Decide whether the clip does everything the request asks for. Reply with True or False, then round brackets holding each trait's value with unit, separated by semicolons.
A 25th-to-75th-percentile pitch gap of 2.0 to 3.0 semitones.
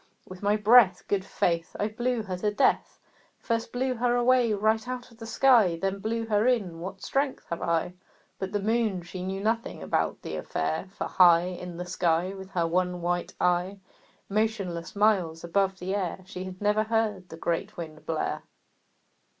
False (3.8 semitones)